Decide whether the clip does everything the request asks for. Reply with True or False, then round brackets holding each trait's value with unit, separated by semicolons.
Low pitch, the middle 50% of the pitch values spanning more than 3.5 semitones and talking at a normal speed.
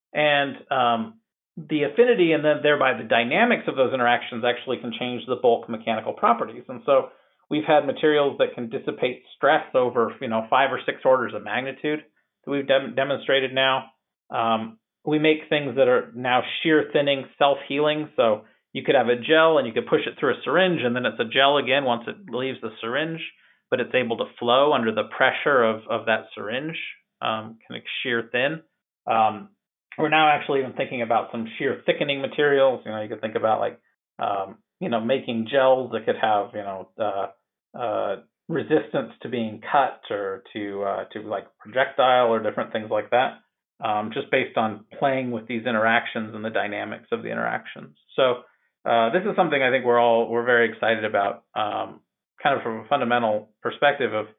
True (130 Hz; 4.6 semitones; 195 wpm)